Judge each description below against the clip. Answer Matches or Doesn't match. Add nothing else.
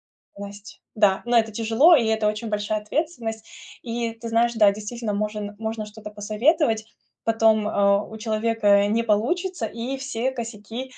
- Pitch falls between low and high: Doesn't match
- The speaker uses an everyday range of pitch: Doesn't match